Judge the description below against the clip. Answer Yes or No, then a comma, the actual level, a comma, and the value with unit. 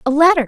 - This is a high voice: Yes, very high, 300 Hz